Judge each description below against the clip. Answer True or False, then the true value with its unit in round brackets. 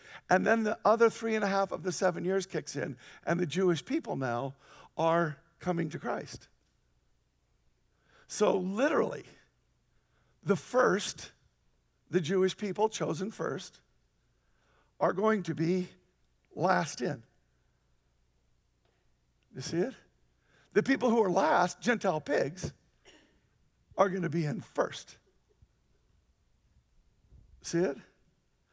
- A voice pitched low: False (170 Hz)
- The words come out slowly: True (115 wpm)